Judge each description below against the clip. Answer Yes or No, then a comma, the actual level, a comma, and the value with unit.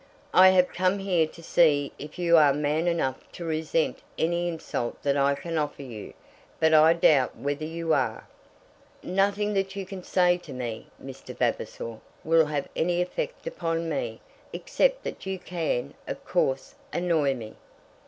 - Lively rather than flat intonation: No, average, 3.8 semitones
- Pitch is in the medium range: Yes, medium, 165 Hz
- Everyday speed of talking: Yes, average, 165 wpm